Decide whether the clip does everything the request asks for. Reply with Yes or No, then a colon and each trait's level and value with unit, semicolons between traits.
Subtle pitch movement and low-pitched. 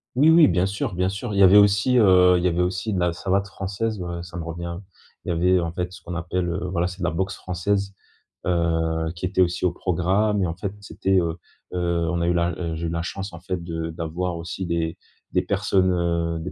Yes: narrow, 2.1 semitones; very low, 90 Hz